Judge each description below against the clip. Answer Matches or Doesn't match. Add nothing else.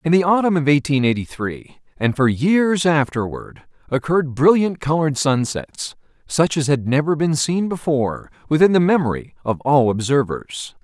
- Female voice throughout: Doesn't match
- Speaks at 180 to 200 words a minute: Doesn't match